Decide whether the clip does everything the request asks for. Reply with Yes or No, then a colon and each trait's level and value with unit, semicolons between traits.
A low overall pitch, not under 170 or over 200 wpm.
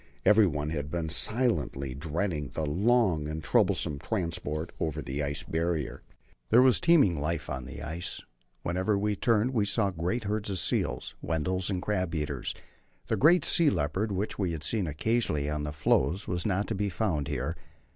Yes: very low, 85 Hz; average, 175 wpm